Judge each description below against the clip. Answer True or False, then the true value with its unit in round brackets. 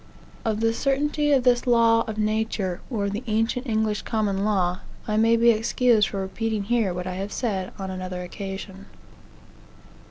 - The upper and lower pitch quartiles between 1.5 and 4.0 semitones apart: True (3.0 semitones)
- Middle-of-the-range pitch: False (215 Hz)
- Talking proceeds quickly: False (165 wpm)